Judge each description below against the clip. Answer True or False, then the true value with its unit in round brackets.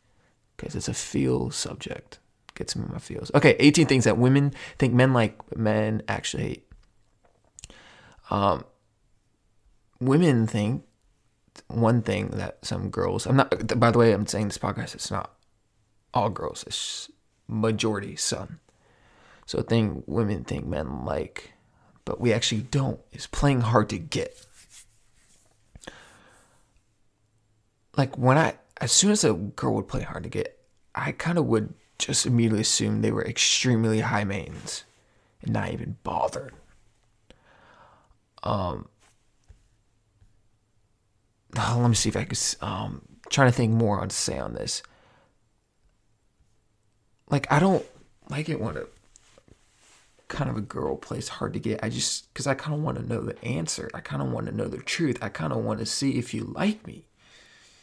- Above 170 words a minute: False (155 wpm)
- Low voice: True (110 Hz)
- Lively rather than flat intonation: False (2.8 semitones)